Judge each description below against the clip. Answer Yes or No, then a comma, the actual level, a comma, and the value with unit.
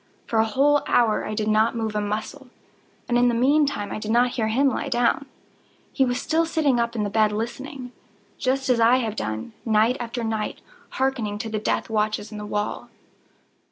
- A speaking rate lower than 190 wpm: No, average, 195 wpm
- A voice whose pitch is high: Yes, high, 230 Hz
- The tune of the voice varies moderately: Yes, average, 3.2 semitones